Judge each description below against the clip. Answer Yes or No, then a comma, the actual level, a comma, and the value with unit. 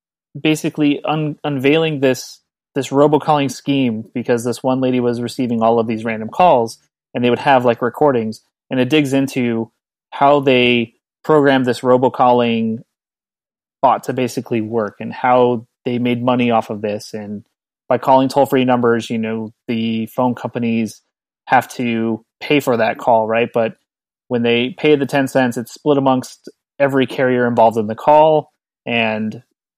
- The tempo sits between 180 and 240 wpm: No, average, 160 wpm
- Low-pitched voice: Yes, low, 125 Hz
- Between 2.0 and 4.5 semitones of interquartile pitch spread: Yes, average, 3.1 semitones